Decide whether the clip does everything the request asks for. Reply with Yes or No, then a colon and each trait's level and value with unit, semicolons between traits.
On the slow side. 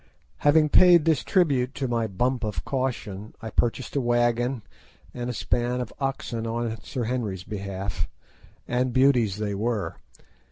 No: average, 150 wpm